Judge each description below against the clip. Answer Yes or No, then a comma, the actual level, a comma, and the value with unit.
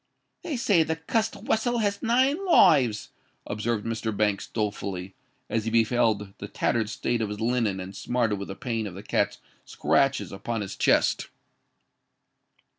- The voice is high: No, low, 115 Hz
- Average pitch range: No, wide, 7.7 semitones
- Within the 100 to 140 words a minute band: No, average, 155 wpm